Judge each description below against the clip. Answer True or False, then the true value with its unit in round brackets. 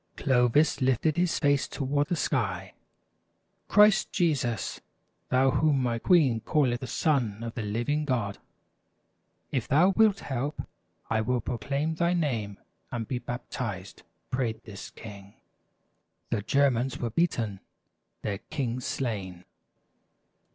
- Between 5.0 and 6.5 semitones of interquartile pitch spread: False (4.6 semitones)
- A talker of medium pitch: False (125 Hz)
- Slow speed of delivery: True (130 wpm)